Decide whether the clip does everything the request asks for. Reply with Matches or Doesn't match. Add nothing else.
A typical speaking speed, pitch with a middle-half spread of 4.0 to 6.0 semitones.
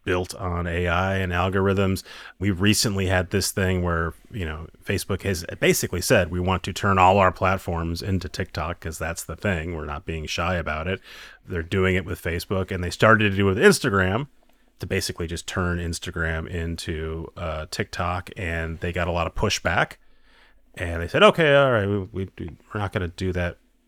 Doesn't match